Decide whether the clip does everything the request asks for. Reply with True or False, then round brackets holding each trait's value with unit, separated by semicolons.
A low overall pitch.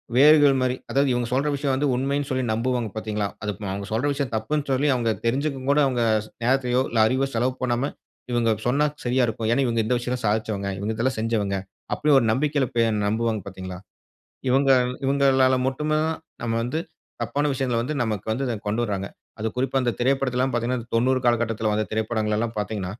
True (125 Hz)